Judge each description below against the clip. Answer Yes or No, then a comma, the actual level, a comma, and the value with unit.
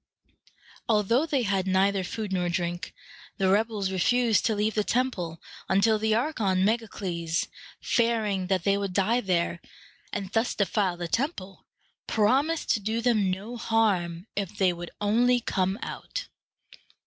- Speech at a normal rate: Yes, average, 150 wpm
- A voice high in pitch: Yes, high, 205 Hz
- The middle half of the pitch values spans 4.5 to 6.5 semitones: No, average, 3.3 semitones